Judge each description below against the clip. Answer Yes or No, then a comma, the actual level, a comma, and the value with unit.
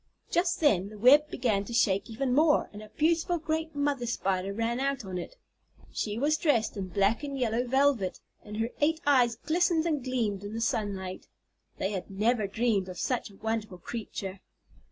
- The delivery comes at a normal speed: Yes, average, 185 wpm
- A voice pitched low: No, high, 230 Hz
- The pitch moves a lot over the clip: Yes, wide, 5.9 semitones